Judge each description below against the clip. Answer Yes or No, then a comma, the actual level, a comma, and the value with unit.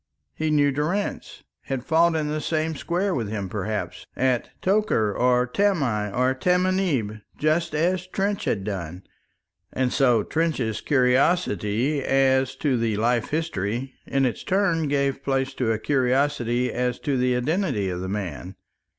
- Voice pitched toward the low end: Yes, low, 130 Hz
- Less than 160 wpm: Yes, average, 150 wpm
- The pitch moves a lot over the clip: Yes, wide, 5.9 semitones